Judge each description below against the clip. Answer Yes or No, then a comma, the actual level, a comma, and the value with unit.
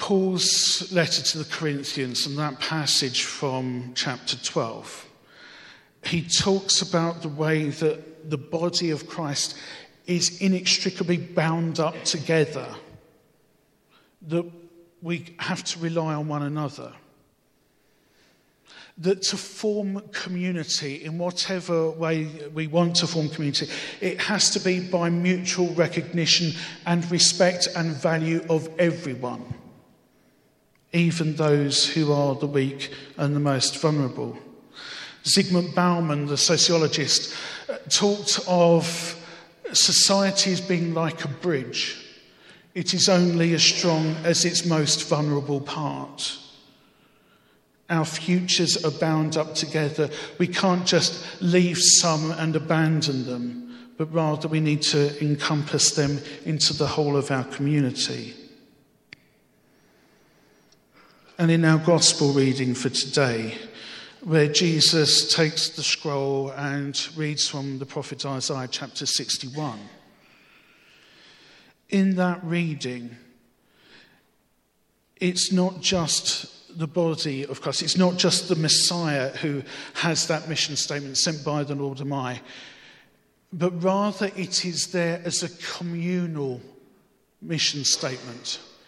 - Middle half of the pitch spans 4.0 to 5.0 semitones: No, average, 3.1 semitones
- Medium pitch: Yes, medium, 160 Hz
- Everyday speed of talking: No, slow, 115 wpm